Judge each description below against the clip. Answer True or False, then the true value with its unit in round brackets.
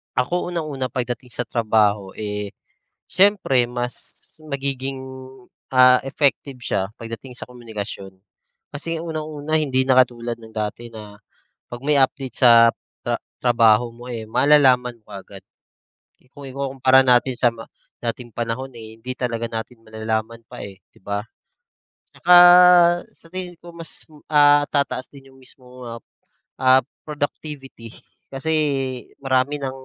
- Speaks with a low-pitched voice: True (125 Hz)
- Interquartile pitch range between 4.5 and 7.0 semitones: False (3.3 semitones)